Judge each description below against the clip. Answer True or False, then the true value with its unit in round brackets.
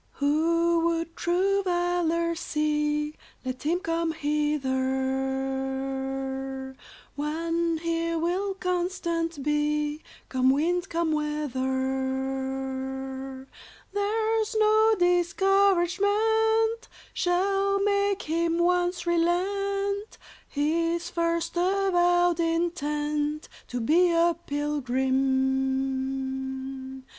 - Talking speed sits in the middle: False (75 wpm)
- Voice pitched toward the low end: False (330 Hz)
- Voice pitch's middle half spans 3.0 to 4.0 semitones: False (4.8 semitones)